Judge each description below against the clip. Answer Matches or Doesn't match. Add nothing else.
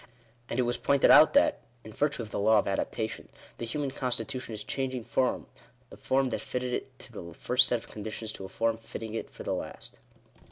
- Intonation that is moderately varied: Matches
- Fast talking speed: Matches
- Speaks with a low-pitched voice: Matches